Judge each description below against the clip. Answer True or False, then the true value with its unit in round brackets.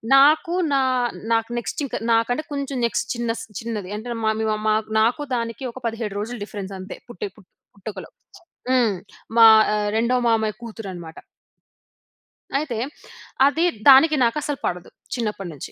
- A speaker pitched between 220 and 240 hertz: True (230 Hz)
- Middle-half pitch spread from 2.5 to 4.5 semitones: True (3.1 semitones)